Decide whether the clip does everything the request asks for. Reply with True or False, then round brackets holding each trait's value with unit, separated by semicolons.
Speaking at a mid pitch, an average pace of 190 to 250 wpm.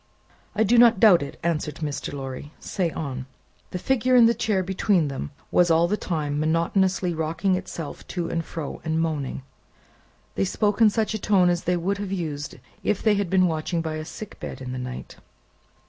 True (170 Hz; 195 wpm)